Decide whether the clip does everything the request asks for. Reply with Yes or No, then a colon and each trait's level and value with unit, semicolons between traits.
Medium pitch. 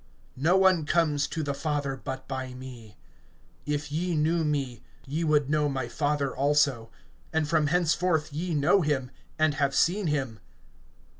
Yes: medium, 145 Hz